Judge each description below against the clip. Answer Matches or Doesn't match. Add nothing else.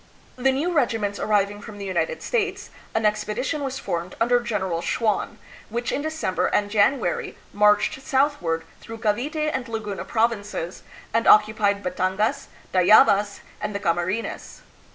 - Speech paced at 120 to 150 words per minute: Matches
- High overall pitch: Matches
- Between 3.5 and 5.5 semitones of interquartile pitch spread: Matches